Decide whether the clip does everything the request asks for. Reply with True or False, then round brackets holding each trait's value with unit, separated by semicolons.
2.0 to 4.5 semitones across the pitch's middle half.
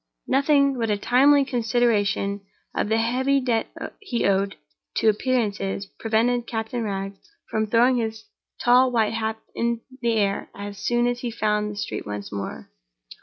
True (3.0 semitones)